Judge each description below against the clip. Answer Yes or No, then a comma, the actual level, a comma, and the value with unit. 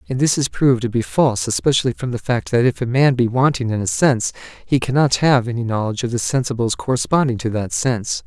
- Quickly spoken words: Yes, fast, 230 wpm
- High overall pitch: No, low, 125 Hz